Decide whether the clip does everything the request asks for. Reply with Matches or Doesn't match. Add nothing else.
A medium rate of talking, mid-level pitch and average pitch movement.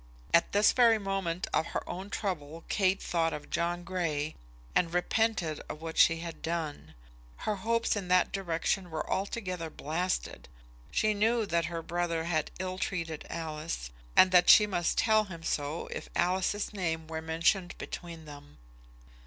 Matches